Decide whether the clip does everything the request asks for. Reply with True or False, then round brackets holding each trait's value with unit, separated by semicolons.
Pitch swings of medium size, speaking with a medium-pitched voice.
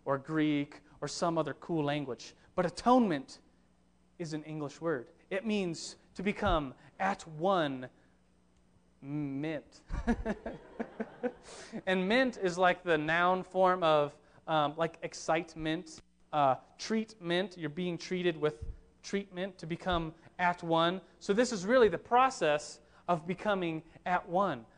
True (3.8 semitones; 165 Hz)